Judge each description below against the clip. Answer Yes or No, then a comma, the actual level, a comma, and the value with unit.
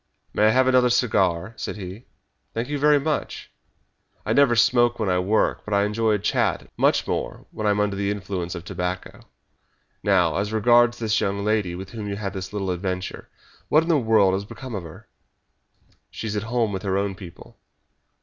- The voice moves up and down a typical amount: Yes, average, 3.5 semitones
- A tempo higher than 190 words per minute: Yes, average, 200 wpm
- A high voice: No, low, 105 Hz